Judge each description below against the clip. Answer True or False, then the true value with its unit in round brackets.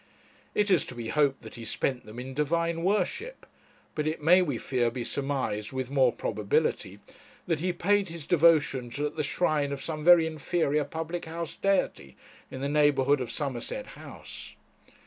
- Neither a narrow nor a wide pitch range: True (4.5 semitones)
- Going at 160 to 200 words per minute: True (170 wpm)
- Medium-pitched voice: True (145 Hz)